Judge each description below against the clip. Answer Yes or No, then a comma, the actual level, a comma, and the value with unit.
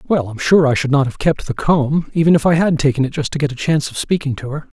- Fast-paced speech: Yes, fast, 315 wpm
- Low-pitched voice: No, medium, 145 Hz